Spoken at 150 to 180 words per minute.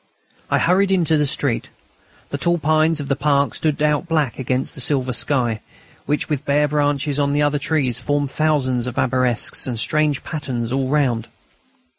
Yes: average, 175 wpm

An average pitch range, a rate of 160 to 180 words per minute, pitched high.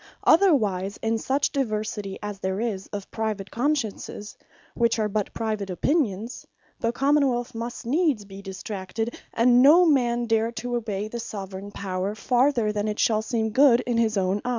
Yes: average, 3.1 semitones; average, 170 wpm; high, 225 Hz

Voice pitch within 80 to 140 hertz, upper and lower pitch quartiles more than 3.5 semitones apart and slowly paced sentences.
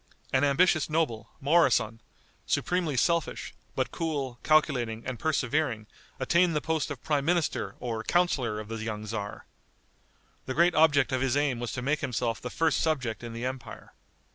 No: low, 135 Hz; average, 5.1 semitones; average, 165 wpm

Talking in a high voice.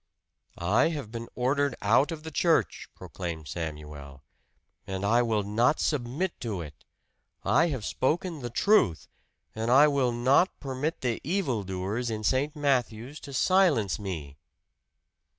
No: low, 120 Hz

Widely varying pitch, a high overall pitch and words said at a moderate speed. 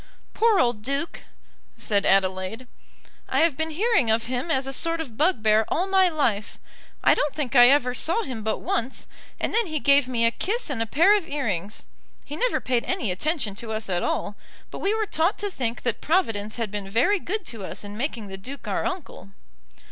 No: wide, 7.2 semitones; very high, 260 Hz; fast, 210 wpm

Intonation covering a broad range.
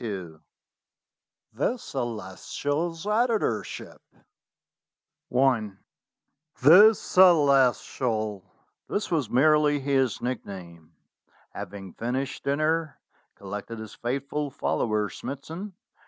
Yes: wide, 6.1 semitones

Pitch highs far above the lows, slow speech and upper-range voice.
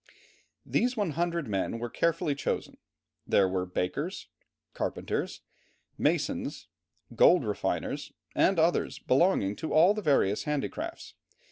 No: wide, 8.1 semitones; slow, 110 wpm; medium, 155 Hz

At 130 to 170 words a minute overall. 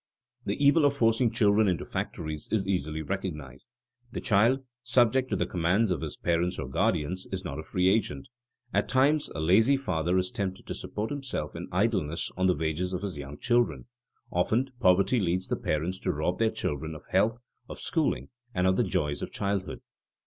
No: average, 190 wpm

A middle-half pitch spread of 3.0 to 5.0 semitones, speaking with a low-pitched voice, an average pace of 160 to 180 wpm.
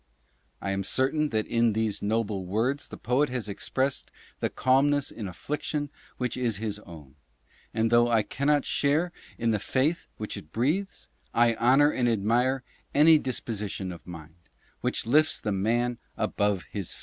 Yes: average, 4.6 semitones; low, 115 Hz; average, 165 wpm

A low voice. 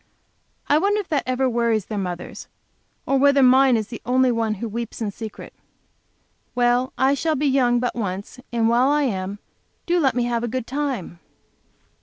No: high, 245 Hz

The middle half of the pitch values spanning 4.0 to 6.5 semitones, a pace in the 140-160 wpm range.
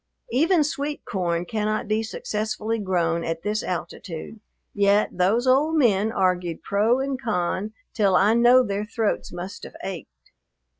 Yes: average, 4.3 semitones; average, 145 wpm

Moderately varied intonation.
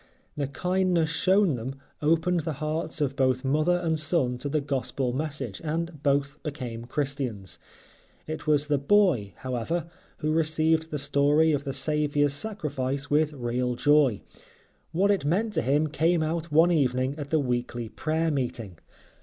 Yes: average, 3.3 semitones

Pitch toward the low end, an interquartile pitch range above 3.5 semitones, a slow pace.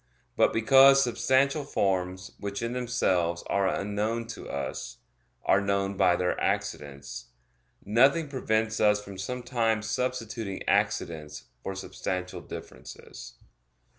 Yes: low, 105 Hz; average, 4.2 semitones; slow, 110 wpm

